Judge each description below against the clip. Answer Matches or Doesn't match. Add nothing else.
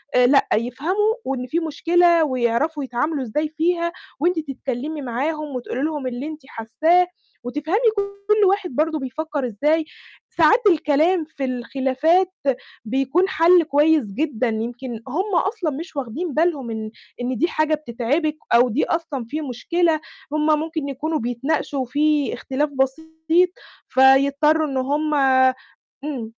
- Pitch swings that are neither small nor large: Matches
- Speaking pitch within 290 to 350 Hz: Matches